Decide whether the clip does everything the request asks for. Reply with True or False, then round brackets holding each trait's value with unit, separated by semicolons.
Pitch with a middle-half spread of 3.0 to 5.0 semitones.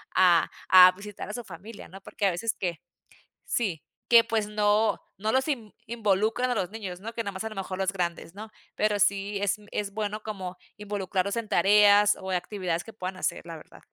False (2.5 semitones)